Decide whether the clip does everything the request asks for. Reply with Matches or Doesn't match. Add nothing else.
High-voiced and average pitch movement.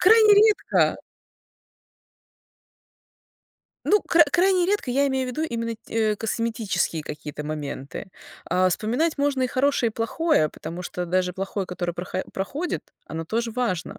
Doesn't match